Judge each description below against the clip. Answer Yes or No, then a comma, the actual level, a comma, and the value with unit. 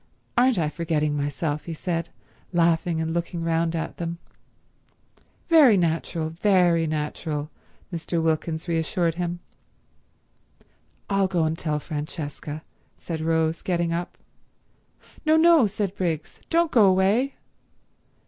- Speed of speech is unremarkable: No, slow, 120 wpm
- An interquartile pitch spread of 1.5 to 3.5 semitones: Yes, average, 2.7 semitones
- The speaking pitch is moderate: Yes, medium, 170 Hz